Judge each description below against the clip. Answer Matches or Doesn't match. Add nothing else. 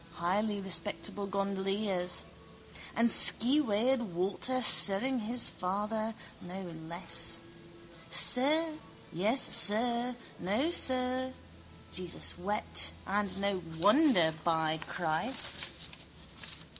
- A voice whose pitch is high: Matches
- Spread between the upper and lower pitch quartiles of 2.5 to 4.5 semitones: Doesn't match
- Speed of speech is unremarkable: Doesn't match